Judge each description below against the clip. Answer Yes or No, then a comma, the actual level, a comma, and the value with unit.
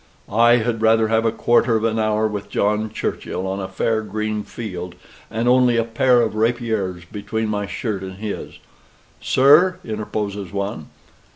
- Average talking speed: Yes, average, 170 wpm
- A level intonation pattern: Yes, narrow, 2.1 semitones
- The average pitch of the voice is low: Yes, low, 110 Hz